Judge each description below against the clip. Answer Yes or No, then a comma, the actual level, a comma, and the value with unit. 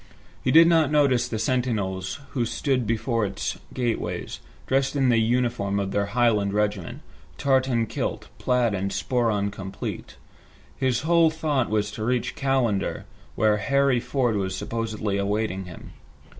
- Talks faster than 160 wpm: No, average, 145 wpm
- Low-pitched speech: Yes, low, 115 Hz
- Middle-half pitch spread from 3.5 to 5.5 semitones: Yes, average, 4.3 semitones